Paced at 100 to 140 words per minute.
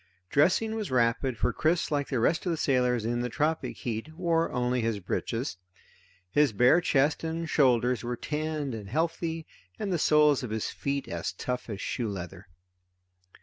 No: average, 180 wpm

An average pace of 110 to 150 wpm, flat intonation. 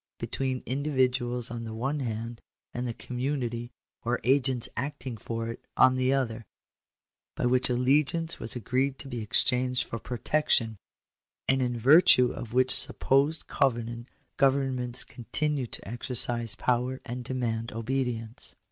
Yes: average, 140 wpm; narrow, 2.1 semitones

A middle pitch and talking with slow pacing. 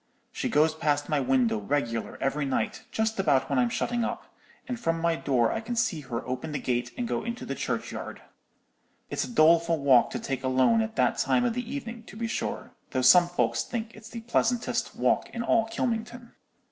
No: medium, 170 Hz; fast, 205 wpm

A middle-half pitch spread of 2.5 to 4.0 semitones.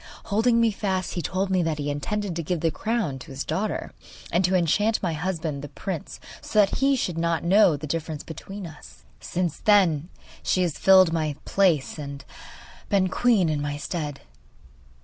No: average, 4.4 semitones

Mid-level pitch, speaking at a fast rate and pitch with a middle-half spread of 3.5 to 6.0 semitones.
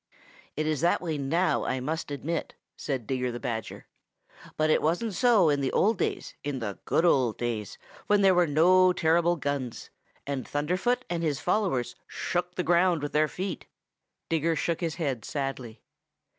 No: medium, 155 Hz; average, 170 wpm; average, 4.6 semitones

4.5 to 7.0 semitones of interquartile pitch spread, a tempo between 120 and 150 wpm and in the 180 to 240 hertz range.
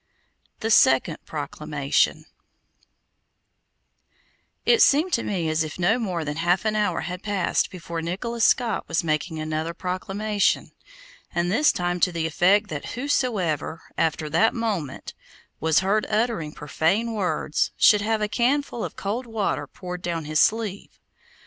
Yes: average, 5.1 semitones; average, 145 wpm; high, 190 Hz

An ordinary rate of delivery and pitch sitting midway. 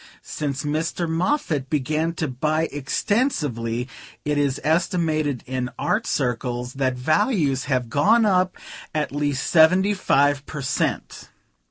No: slow, 125 wpm; medium, 150 Hz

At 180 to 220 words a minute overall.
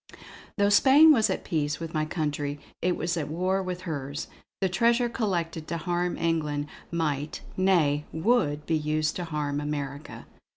No: average, 160 wpm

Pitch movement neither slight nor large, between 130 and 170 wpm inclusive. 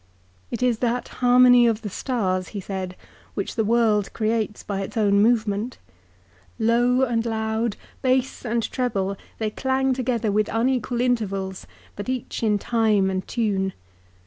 Yes: average, 3.1 semitones; average, 165 wpm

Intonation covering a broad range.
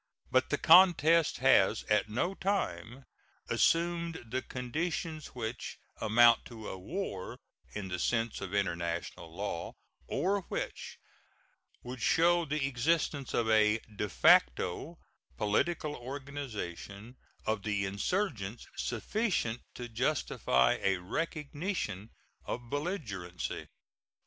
Yes: wide, 7.7 semitones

